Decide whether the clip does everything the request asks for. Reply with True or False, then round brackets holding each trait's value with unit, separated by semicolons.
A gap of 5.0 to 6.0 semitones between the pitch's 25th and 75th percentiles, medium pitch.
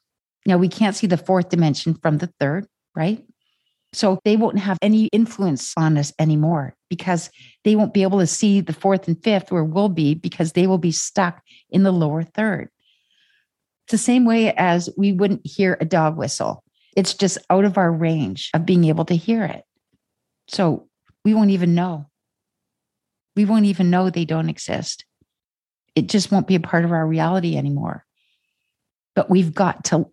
False (3.6 semitones; 180 Hz)